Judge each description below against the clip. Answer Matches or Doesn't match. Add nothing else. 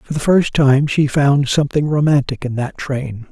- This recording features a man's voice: Matches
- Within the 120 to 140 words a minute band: Doesn't match